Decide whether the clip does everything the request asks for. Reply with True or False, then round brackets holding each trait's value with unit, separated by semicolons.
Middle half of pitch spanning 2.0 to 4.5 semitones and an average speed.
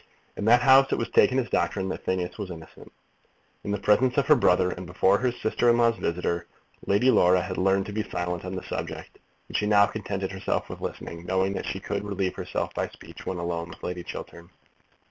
False (3.4 semitones; 220 wpm)